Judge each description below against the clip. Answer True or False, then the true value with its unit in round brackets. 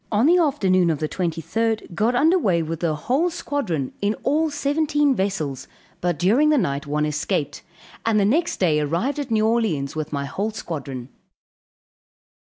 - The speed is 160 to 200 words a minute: True (165 wpm)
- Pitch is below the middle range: False (200 Hz)